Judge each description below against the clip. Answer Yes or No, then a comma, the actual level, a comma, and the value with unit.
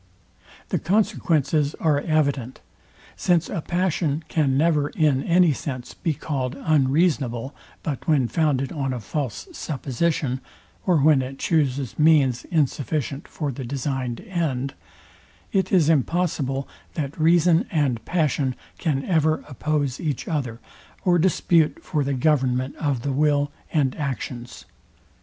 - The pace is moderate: No, slow, 130 wpm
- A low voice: No, medium, 145 Hz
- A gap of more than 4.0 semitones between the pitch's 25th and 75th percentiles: No, average, 3.4 semitones